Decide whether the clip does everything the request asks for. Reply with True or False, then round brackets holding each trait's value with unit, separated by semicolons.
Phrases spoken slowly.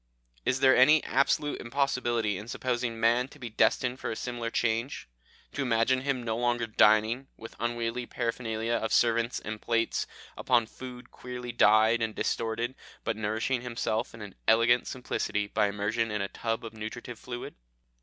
False (160 wpm)